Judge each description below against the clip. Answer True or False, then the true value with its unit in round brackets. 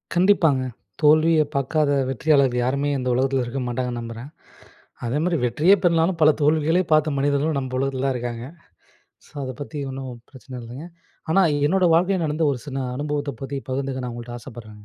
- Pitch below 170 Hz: True (140 Hz)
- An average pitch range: True (3.4 semitones)